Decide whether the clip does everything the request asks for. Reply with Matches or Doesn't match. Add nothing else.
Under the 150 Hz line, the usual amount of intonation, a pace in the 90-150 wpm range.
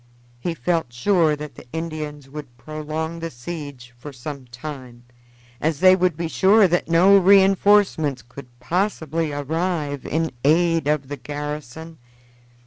Doesn't match